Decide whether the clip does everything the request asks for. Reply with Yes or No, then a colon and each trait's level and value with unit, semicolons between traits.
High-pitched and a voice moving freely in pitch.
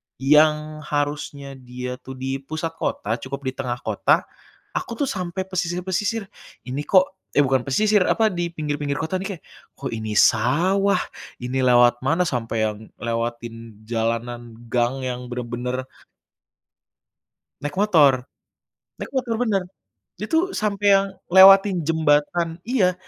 No: medium, 145 Hz; wide, 6.8 semitones